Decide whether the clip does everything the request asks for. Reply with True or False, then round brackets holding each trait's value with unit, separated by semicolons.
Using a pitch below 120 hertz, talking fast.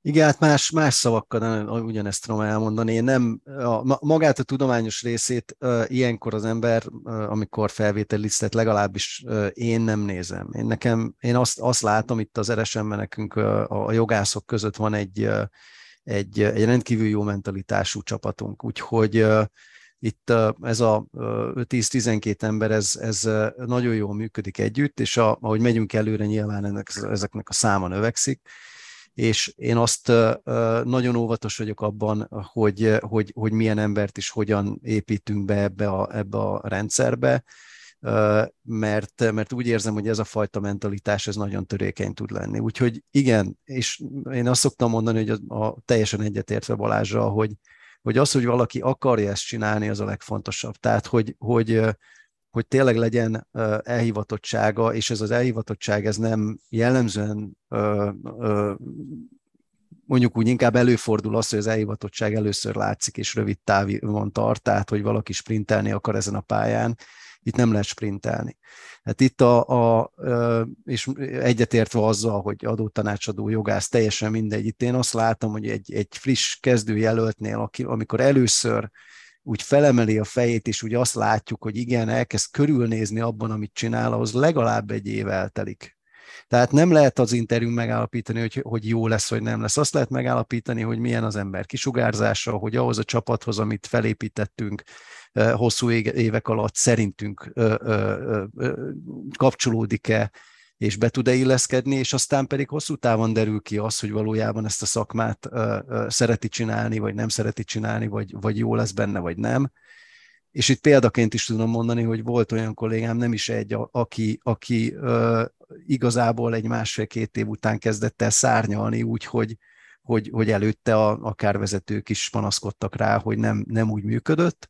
True (110 Hz; 160 wpm)